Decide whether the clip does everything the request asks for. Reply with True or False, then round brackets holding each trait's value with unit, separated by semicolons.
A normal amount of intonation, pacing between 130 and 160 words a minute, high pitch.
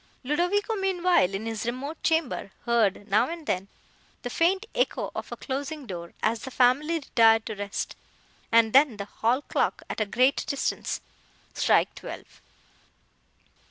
False (6.3 semitones; 150 wpm; 255 Hz)